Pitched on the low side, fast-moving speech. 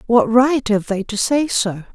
No: high, 230 Hz; fast, 215 wpm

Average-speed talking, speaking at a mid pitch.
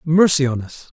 Yes: average, 180 wpm; medium, 145 Hz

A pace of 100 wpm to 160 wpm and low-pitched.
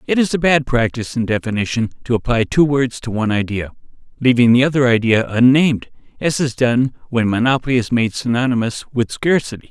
No: average, 180 wpm; low, 125 Hz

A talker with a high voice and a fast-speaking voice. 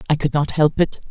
No: medium, 150 Hz; fast, 270 wpm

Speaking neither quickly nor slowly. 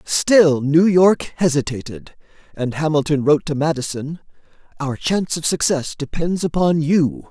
No: slow, 130 wpm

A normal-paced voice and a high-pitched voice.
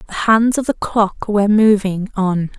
Yes: average, 185 wpm; high, 205 Hz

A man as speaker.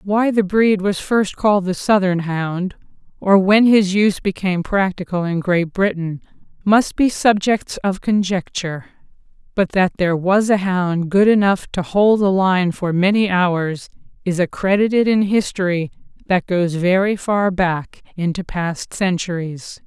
No: female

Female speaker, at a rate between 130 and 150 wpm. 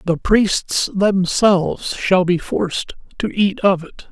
No: male; average, 145 wpm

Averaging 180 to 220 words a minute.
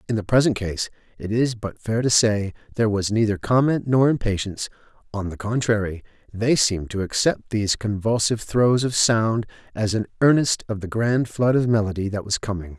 Yes: average, 190 wpm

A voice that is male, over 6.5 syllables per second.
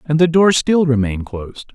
No: male; 5.7 syllables/s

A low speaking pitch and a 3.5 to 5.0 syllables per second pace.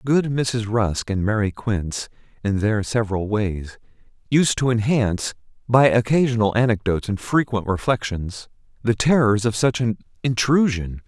Yes: low, 115 Hz; 4.7 syllables/s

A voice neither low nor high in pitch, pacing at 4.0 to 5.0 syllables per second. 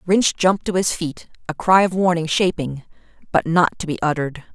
No: medium, 170 Hz; 5.6 syllables/s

